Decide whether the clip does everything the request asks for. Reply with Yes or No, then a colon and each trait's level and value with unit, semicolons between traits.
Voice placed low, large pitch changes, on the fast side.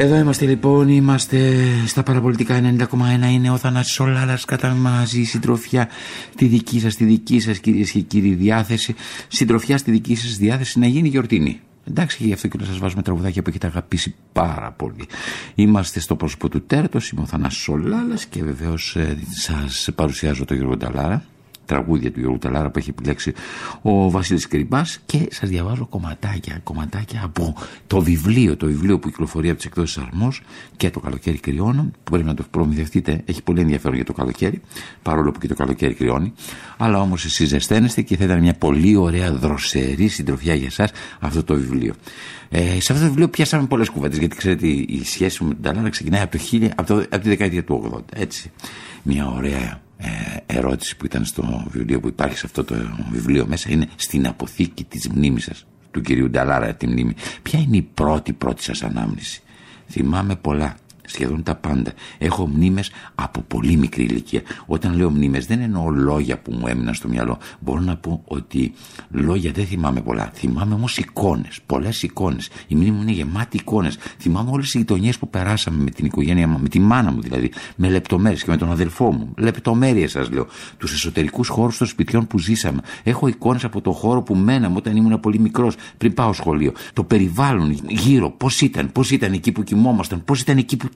Yes: very low, 95 Hz; wide, 7.2 semitones; fast, 185 wpm